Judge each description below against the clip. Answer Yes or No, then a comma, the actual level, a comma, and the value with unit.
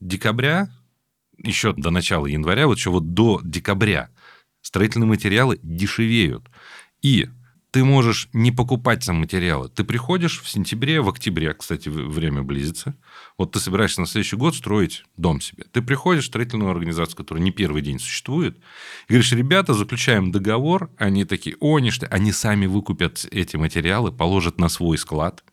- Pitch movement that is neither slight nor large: No, wide, 5.9 semitones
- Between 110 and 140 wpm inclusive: No, average, 155 wpm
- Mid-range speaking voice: No, low, 105 Hz